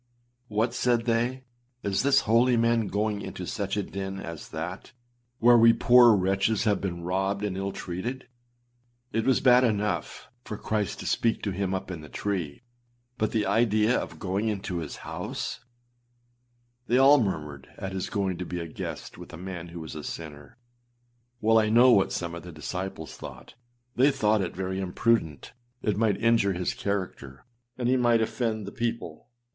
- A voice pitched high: No, low, 100 Hz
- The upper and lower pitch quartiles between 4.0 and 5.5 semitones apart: Yes, average, 4.3 semitones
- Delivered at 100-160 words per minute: No, average, 180 wpm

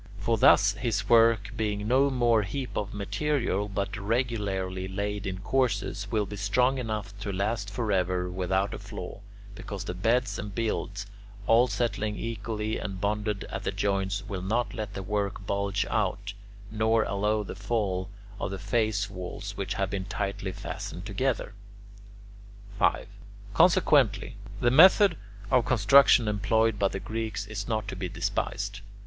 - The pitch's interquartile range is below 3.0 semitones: Yes, narrow, 2.4 semitones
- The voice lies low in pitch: Yes, low, 105 Hz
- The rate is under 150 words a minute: No, average, 155 wpm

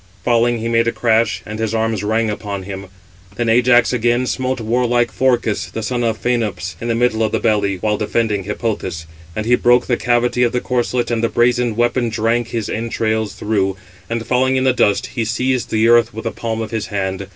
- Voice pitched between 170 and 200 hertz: No, low, 115 Hz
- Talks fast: Yes, fast, 210 wpm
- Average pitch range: No, narrow, 1.9 semitones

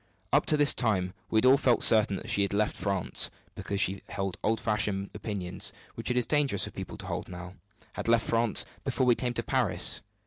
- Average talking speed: No, fast, 215 wpm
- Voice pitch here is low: Yes, low, 110 Hz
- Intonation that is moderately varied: Yes, average, 3.7 semitones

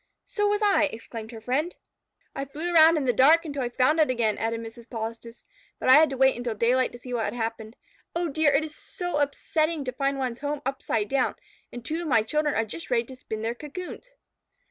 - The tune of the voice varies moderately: Yes, average, 4.9 semitones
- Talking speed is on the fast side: Yes, fast, 230 wpm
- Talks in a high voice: Yes, very high, 265 Hz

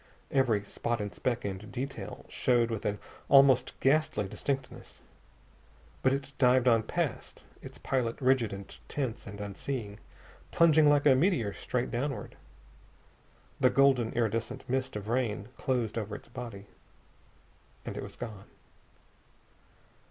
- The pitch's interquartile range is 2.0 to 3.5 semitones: No, average, 3.9 semitones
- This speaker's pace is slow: Yes, slow, 130 wpm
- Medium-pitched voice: No, low, 120 Hz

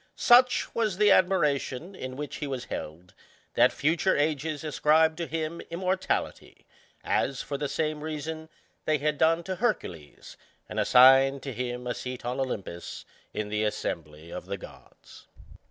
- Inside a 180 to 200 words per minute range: No, average, 155 wpm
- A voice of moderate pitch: Yes, medium, 150 Hz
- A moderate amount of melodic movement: Yes, average, 4.4 semitones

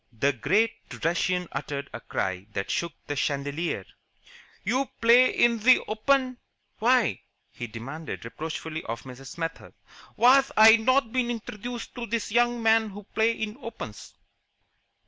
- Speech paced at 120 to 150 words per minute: Yes, average, 140 wpm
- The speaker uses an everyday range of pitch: No, wide, 8.6 semitones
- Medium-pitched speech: No, high, 215 Hz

